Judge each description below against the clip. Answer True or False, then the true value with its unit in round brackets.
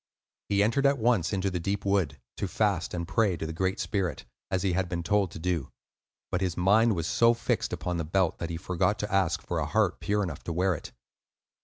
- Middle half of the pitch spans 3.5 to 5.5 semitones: False (3.1 semitones)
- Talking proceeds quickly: True (230 wpm)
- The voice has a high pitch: False (95 Hz)